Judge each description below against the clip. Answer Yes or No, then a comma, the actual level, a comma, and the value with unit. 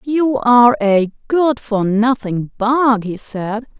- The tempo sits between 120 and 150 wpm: Yes, average, 140 wpm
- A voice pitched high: Yes, high, 230 Hz